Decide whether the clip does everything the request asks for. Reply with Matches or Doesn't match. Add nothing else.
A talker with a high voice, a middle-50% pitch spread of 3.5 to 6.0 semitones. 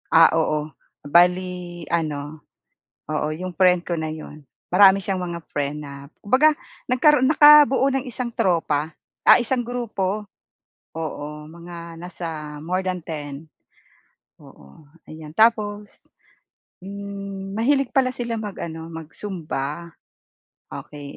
Doesn't match